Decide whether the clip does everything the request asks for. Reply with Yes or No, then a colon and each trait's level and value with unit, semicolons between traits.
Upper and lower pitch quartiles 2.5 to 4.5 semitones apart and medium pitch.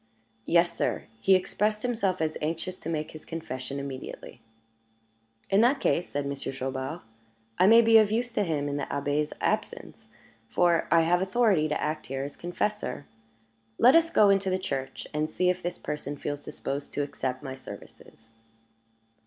No: average, 5.2 semitones; medium, 165 Hz